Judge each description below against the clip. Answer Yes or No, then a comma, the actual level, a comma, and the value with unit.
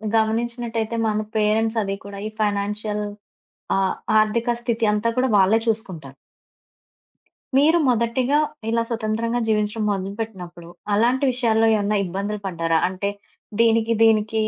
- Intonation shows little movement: Yes, narrow, 2.3 semitones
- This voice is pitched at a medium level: No, high, 220 Hz